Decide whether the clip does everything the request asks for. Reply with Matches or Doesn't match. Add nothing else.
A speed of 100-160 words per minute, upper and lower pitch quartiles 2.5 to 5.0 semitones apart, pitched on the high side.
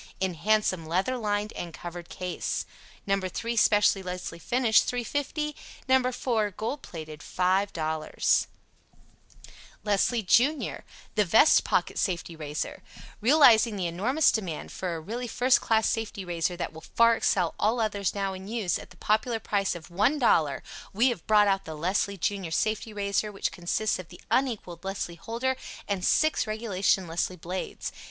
Matches